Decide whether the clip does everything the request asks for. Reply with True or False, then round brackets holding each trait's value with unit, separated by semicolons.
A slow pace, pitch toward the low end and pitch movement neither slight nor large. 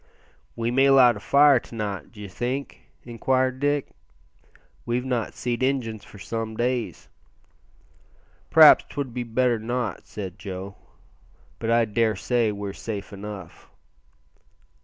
True (125 wpm; 115 Hz; 3.3 semitones)